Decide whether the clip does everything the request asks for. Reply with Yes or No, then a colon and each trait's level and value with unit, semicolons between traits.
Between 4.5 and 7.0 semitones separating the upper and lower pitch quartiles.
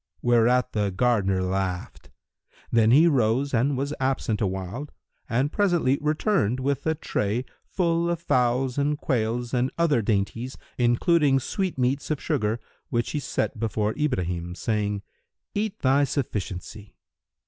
Yes: average, 5.1 semitones